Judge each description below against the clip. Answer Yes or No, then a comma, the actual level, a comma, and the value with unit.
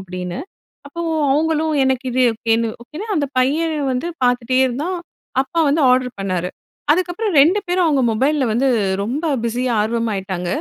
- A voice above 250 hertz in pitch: Yes, very high, 260 Hz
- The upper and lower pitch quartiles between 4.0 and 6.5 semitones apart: Yes, wide, 5.5 semitones